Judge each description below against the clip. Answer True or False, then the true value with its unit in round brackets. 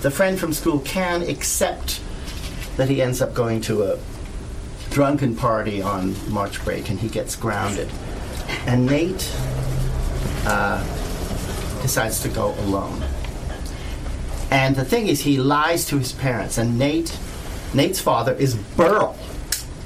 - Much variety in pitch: True (8.2 semitones)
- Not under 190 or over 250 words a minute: False (135 wpm)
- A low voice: True (115 Hz)